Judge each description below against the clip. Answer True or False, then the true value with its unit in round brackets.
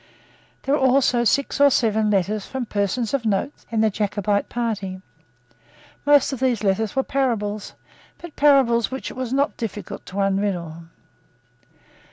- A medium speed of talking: True (150 wpm)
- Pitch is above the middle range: True (225 Hz)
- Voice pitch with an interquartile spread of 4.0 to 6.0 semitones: True (4.5 semitones)